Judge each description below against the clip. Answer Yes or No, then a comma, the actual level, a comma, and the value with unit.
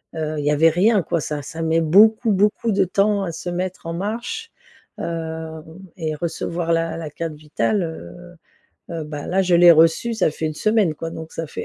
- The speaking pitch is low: No, medium, 165 Hz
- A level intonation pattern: No, average, 3.2 semitones